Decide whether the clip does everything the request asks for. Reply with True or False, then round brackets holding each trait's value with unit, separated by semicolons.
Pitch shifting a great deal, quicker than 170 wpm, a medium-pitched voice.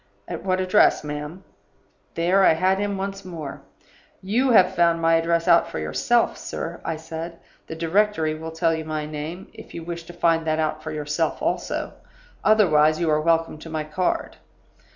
False (2.9 semitones; 180 wpm; 165 Hz)